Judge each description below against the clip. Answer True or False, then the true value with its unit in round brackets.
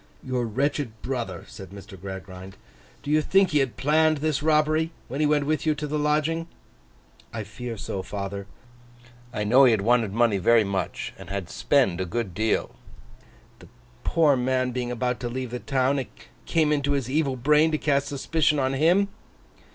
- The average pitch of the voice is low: True (130 Hz)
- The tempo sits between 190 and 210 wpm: False (180 wpm)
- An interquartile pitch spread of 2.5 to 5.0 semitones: False (5.4 semitones)